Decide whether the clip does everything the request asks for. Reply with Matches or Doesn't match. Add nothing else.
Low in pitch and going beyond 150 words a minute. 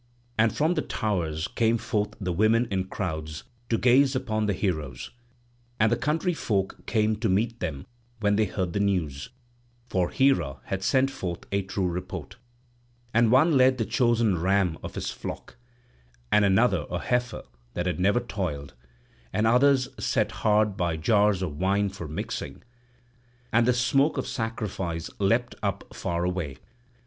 Matches